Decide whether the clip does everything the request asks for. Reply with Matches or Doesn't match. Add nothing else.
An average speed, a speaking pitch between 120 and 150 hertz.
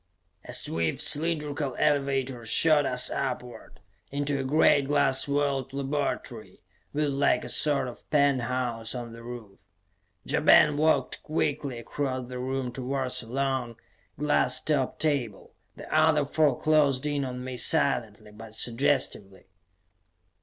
Doesn't match